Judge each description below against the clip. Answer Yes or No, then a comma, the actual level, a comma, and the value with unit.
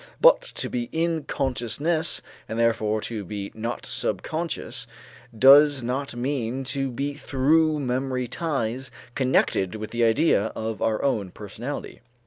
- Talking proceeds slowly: Yes, slow, 130 wpm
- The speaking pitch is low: Yes, low, 125 Hz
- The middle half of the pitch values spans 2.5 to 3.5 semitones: No, average, 4.2 semitones